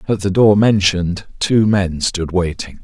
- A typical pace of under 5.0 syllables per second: Yes, 4.3 syllables/s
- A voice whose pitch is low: Yes, very low, 95 Hz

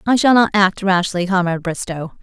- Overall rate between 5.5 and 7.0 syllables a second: Yes, 5.6 syllables/s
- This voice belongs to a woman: Yes, female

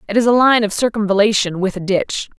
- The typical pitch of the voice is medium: No, high, 210 Hz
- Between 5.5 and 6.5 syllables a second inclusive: Yes, 6.1 syllables/s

